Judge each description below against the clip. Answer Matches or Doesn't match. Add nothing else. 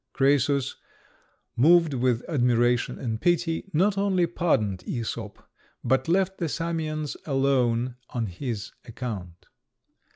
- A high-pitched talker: Doesn't match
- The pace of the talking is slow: Matches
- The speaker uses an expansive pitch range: Matches